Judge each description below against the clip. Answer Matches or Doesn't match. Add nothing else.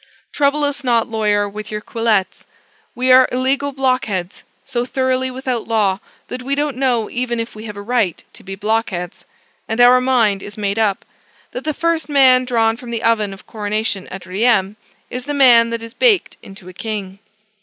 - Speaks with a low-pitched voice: Doesn't match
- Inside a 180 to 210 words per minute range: Matches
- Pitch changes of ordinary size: Matches